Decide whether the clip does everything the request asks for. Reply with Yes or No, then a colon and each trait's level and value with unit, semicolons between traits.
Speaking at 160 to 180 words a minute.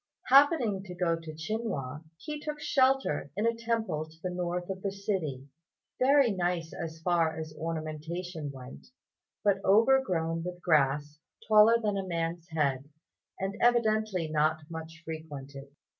No: average, 145 wpm